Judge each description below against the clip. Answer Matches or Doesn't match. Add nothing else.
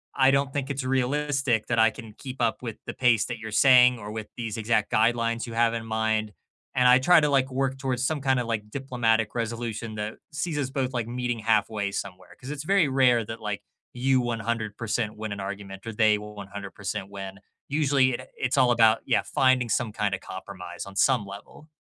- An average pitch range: Matches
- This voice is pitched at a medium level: Doesn't match